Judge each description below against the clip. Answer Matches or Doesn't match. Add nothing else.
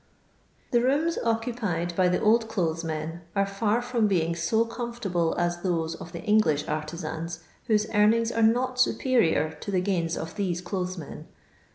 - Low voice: Doesn't match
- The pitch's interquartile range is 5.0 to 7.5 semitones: Matches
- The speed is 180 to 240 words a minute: Doesn't match